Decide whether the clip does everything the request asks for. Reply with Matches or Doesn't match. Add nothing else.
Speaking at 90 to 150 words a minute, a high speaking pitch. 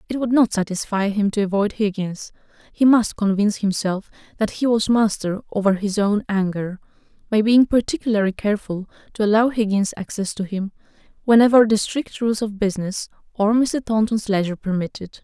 Doesn't match